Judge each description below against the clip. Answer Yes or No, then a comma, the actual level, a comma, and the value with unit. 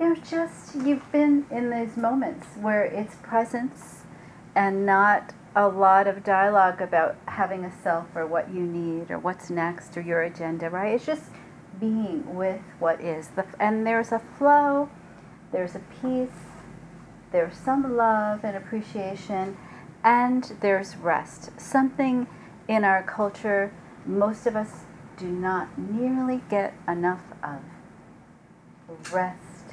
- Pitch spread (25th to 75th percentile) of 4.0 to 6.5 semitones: Yes, average, 4.3 semitones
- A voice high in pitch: Yes, high, 200 Hz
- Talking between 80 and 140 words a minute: Yes, slow, 135 wpm